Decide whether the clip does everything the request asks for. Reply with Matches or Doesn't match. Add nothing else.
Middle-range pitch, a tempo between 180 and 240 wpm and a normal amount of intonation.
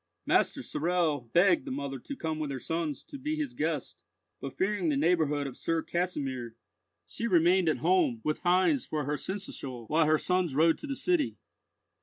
Matches